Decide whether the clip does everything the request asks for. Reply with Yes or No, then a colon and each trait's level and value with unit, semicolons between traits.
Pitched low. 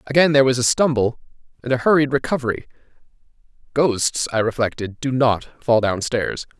Yes: low, 125 Hz